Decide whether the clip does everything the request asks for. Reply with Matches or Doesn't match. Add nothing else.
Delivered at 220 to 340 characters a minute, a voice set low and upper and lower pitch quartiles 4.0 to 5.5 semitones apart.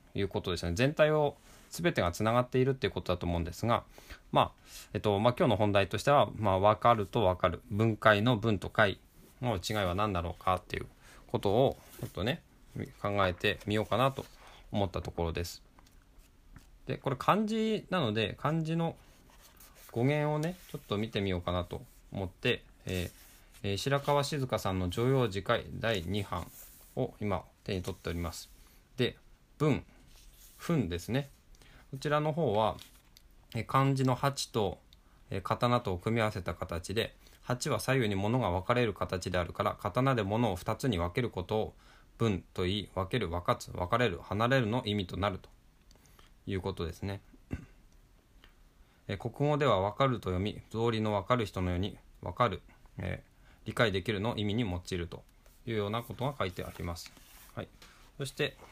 Matches